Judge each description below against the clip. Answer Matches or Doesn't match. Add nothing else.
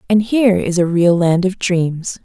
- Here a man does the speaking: Doesn't match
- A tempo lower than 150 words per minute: Doesn't match